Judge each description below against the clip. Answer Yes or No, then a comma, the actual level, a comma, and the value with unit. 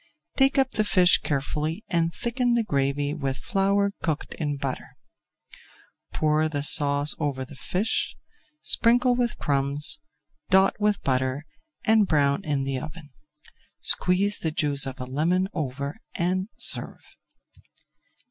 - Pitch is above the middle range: No, medium, 155 Hz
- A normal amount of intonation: No, wide, 5.9 semitones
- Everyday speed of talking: No, slow, 130 wpm